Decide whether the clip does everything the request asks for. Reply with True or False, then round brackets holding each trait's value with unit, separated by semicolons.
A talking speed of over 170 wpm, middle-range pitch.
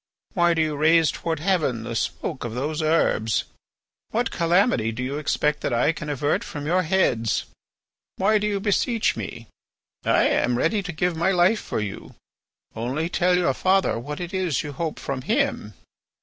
True (180 wpm; 160 Hz)